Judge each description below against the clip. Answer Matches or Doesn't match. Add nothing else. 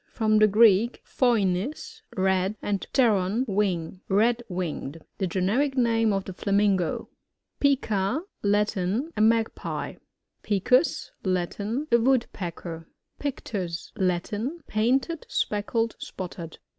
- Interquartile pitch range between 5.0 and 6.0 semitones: Doesn't match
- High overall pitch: Matches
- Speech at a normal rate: Doesn't match